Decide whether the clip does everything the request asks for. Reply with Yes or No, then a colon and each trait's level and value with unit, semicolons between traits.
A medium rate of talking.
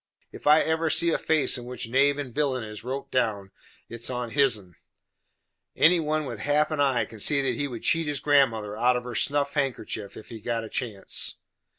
No: fast, 215 wpm